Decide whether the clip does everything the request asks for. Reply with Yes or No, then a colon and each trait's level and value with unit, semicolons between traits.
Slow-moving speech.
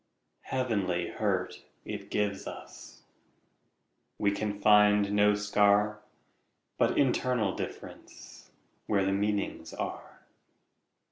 Yes: slow, 75 wpm